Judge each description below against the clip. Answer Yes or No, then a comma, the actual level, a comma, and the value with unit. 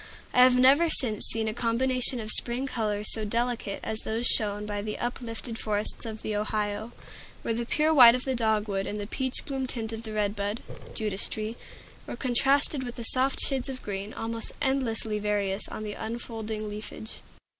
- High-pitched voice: Yes, high, 225 Hz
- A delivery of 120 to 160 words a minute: No, average, 185 wpm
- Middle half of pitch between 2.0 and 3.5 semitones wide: Yes, average, 2.9 semitones